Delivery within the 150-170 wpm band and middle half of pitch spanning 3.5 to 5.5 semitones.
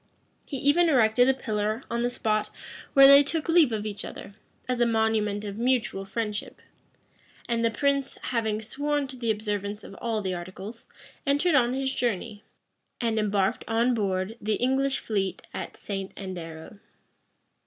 Yes: average, 160 wpm; average, 3.9 semitones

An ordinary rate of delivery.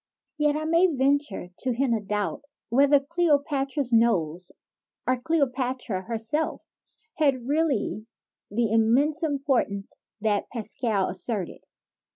No: slow, 115 wpm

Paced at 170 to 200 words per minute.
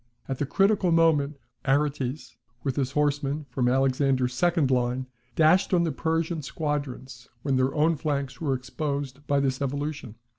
No: average, 150 wpm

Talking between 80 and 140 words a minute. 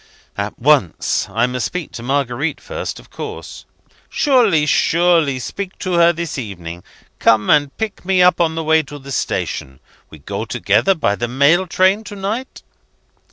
No: average, 165 wpm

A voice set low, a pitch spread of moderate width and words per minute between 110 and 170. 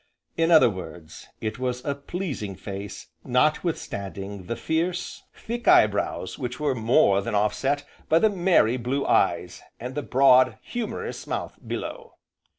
No: low, 130 Hz; wide, 7.4 semitones; average, 145 wpm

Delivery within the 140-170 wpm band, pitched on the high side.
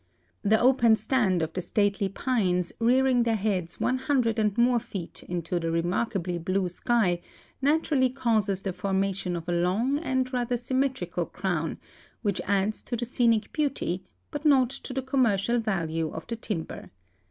Yes: average, 160 wpm; high, 220 Hz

